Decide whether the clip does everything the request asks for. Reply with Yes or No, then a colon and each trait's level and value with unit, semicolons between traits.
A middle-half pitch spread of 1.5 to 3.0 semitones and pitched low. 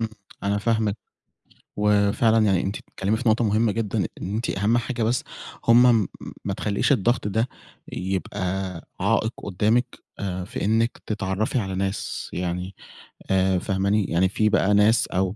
Yes: average, 2.7 semitones; low, 105 Hz